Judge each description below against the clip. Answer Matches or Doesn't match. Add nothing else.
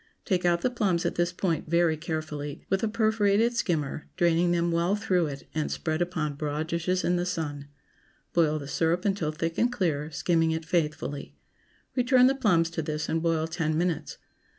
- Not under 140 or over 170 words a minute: Doesn't match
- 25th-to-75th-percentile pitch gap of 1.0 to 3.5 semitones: Matches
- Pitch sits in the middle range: Matches